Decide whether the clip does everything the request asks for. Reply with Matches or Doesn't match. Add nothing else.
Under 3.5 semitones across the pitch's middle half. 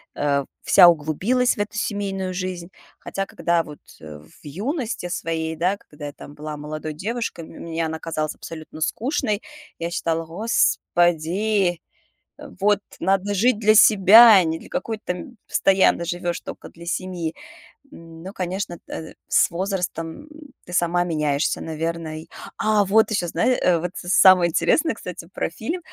Doesn't match